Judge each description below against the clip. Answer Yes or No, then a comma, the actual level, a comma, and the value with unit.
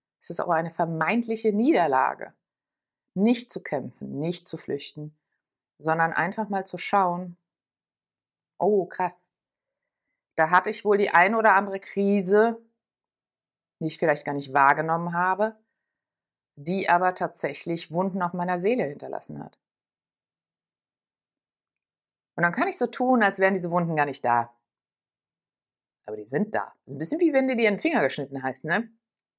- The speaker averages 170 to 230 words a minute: No, average, 150 wpm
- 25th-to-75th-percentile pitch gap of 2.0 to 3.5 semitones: No, average, 5.2 semitones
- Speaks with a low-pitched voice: No, medium, 180 Hz